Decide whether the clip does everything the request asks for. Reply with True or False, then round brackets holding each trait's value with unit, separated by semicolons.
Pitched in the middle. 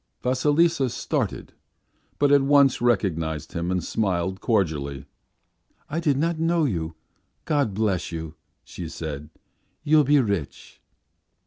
False (110 Hz)